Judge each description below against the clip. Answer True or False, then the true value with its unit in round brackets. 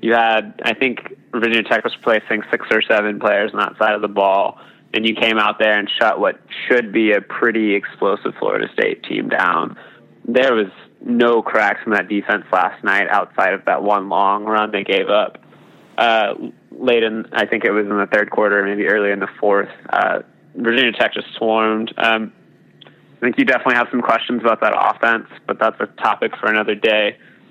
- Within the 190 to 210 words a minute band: True (200 wpm)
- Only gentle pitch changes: True (1.7 semitones)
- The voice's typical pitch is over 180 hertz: False (110 Hz)